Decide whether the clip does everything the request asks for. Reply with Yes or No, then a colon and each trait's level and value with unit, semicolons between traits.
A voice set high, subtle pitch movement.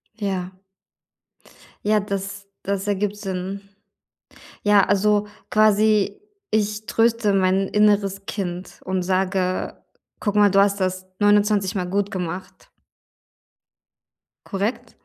Yes: high, 200 Hz; narrow, 1.6 semitones